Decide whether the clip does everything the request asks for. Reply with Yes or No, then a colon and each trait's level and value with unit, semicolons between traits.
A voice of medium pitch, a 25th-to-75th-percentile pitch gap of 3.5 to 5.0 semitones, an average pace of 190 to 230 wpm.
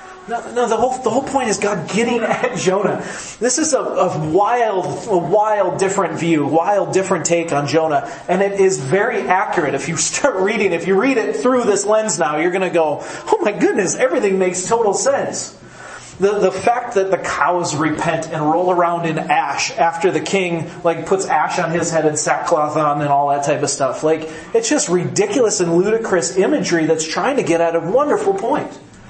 Yes: medium, 180 Hz; average, 4.0 semitones; average, 200 wpm